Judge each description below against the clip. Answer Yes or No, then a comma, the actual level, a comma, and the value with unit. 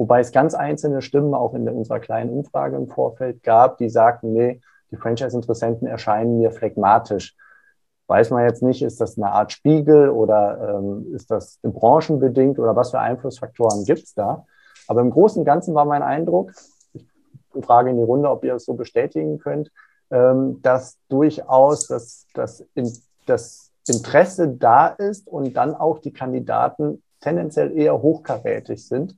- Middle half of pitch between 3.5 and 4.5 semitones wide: Yes, average, 3.8 semitones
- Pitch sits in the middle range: No, low, 130 Hz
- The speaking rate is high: No, average, 165 wpm